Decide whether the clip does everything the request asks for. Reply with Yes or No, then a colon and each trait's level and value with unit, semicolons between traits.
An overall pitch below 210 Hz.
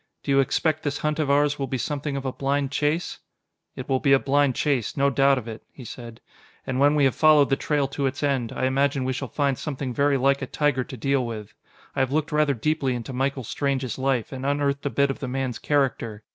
Yes: low, 135 Hz